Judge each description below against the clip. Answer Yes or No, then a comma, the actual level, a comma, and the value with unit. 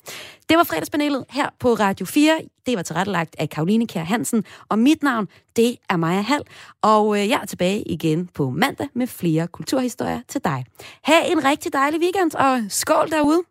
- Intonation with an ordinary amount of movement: No, wide, 7.6 semitones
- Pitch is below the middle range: No, high, 240 Hz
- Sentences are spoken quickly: No, average, 180 wpm